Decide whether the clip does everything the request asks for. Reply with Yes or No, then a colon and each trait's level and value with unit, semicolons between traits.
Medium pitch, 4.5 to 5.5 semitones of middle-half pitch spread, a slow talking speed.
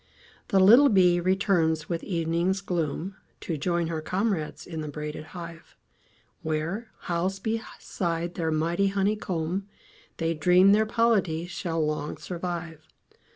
No: medium, 175 Hz; average, 3.0 semitones; slow, 125 wpm